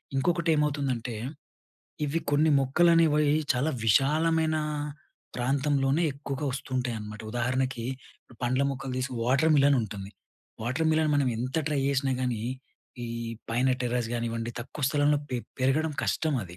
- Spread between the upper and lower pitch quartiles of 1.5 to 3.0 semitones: No, average, 3.4 semitones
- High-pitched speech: No, low, 135 Hz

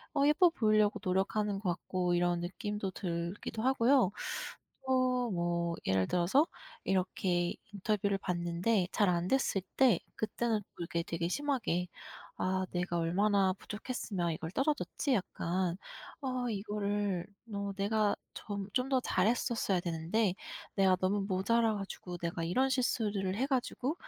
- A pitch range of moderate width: Yes, average, 4.4 semitones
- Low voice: No, high, 195 Hz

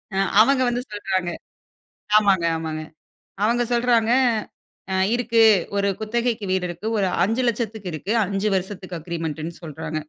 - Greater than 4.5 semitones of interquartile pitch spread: Yes, average, 4.9 semitones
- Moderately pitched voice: No, high, 200 Hz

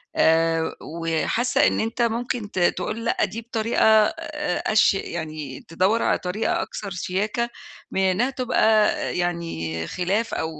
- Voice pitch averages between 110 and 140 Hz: No, high, 210 Hz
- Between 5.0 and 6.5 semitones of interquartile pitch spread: Yes, wide, 5.4 semitones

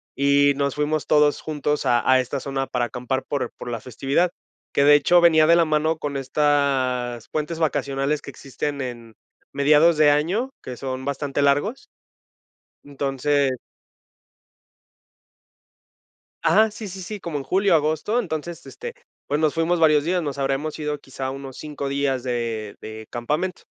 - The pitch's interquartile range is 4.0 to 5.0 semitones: No, average, 2.8 semitones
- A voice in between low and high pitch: Yes, medium, 145 Hz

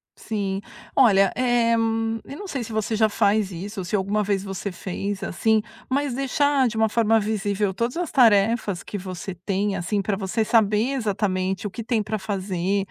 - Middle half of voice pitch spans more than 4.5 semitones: No, average, 2.7 semitones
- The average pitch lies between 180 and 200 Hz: No, high, 210 Hz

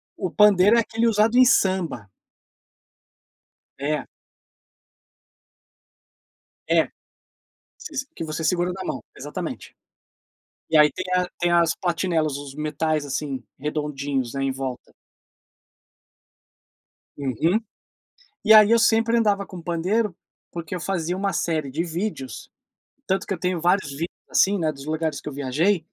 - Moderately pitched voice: Yes, medium, 170 Hz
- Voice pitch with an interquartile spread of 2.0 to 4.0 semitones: No, average, 4.6 semitones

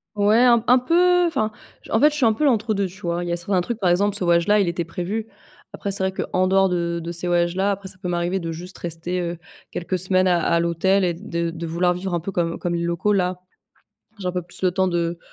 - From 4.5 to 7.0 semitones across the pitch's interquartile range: No, average, 2.8 semitones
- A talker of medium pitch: Yes, medium, 180 Hz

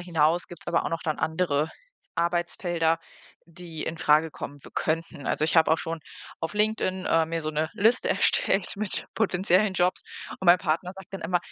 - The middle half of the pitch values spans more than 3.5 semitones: No, narrow, 2.5 semitones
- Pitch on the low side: No, medium, 170 Hz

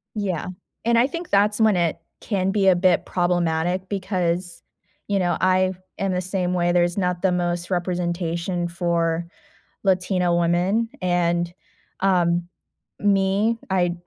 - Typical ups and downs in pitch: No, narrow, 1.9 semitones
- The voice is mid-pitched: Yes, medium, 180 Hz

